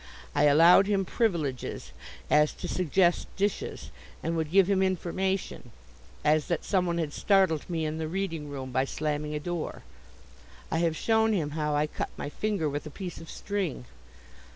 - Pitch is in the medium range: Yes, medium, 165 Hz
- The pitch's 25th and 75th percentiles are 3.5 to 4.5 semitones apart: Yes, average, 4.1 semitones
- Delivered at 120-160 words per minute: No, average, 170 wpm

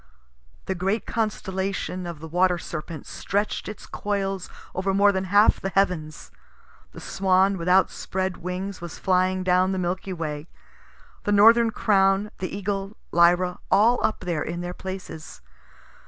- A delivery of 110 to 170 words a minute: Yes, average, 145 wpm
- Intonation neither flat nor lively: No, narrow, 1.7 semitones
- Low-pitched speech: No, high, 190 Hz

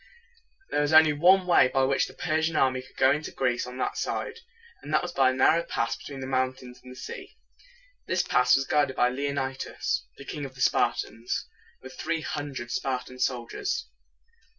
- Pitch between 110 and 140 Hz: Yes, low, 135 Hz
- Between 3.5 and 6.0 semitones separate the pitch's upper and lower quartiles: No, narrow, 2.6 semitones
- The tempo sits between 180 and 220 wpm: Yes, average, 200 wpm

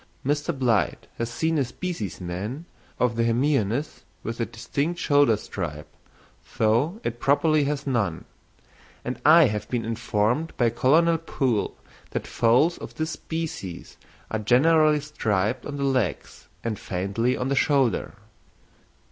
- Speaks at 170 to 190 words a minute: No, slow, 135 wpm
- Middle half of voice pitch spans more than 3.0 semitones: Yes, average, 5.1 semitones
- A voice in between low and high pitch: No, low, 125 Hz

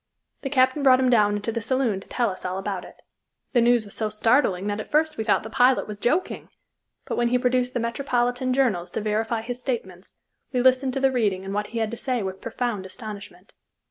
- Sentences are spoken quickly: Yes, fast, 230 wpm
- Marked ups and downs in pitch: No, average, 3.6 semitones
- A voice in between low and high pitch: No, high, 235 Hz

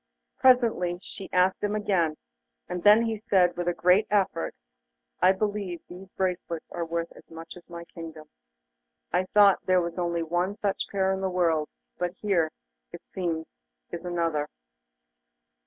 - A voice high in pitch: No, medium, 180 Hz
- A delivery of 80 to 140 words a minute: No, average, 155 wpm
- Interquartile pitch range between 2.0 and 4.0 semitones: Yes, narrow, 2.4 semitones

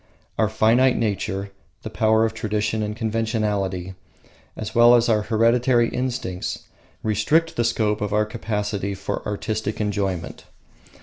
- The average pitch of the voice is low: Yes, low, 110 Hz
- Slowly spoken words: Yes, slow, 130 wpm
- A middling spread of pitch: No, narrow, 1.9 semitones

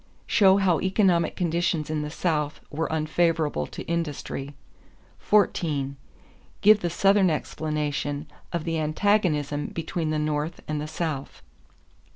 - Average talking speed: No, slow, 125 wpm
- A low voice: No, medium, 160 Hz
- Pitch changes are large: No, average, 2.7 semitones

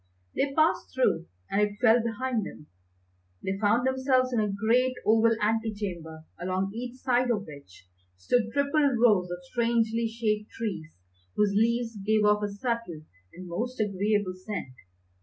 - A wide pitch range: No, average, 3.4 semitones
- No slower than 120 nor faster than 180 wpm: Yes, average, 155 wpm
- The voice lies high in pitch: Yes, high, 220 Hz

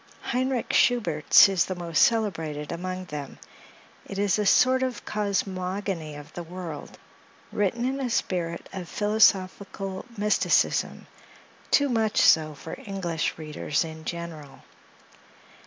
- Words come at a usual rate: No, slow, 120 wpm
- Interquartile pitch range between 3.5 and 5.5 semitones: Yes, average, 4.4 semitones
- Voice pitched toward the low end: No, medium, 185 Hz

